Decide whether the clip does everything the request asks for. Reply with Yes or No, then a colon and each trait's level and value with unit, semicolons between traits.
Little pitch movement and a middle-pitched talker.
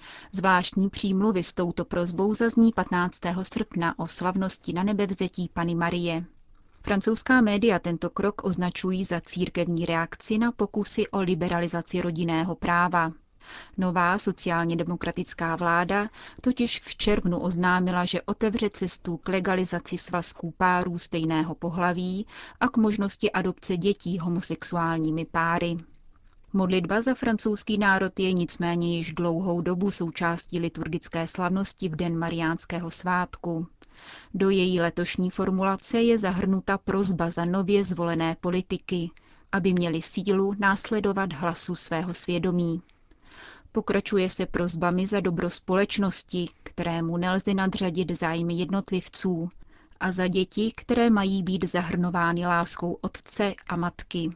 Yes: narrow, 2.3 semitones; medium, 180 Hz